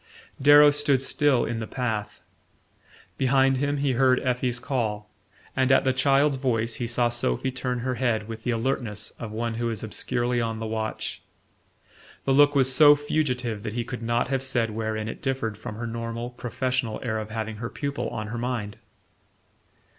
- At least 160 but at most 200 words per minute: Yes, average, 180 wpm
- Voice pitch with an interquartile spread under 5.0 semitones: Yes, average, 2.8 semitones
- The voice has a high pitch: No, low, 120 Hz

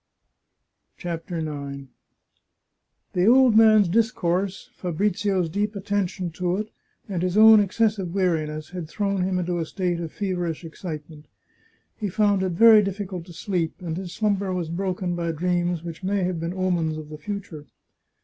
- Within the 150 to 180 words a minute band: Yes, average, 155 wpm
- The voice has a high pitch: No, medium, 180 Hz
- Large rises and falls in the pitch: No, average, 3.1 semitones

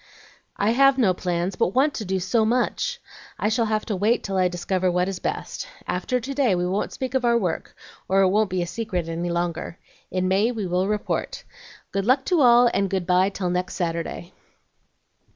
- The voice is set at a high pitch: Yes, high, 195 Hz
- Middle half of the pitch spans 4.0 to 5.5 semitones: Yes, average, 4.5 semitones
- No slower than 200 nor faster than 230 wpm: Yes, fast, 205 wpm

